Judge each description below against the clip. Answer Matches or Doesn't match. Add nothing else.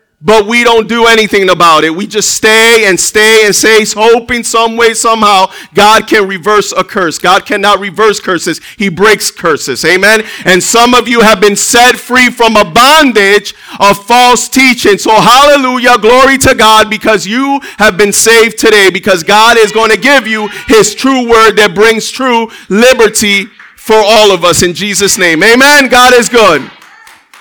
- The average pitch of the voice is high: Matches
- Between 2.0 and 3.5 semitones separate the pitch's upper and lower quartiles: Matches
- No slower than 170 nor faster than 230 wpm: Matches